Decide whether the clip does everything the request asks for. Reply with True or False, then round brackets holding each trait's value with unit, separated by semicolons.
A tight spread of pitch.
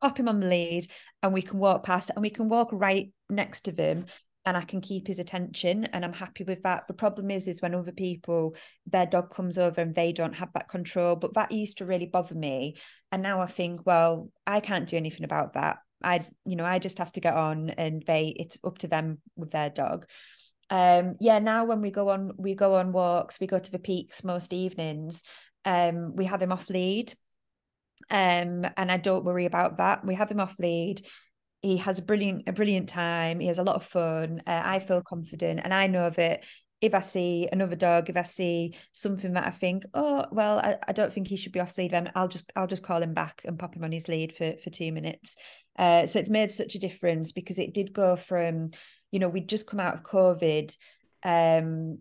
True (2.2 semitones)